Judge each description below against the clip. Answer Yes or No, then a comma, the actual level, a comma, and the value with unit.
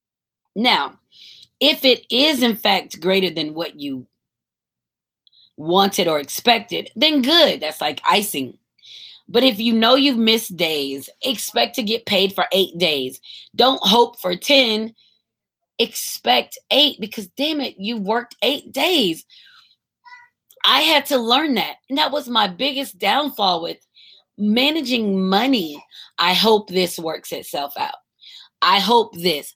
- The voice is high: Yes, high, 225 Hz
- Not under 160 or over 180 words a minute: No, average, 140 wpm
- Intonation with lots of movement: Yes, wide, 6.5 semitones